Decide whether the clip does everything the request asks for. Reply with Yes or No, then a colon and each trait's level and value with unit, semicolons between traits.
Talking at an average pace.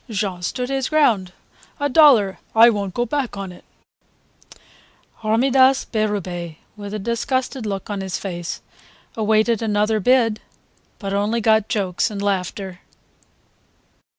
No: slow, 125 wpm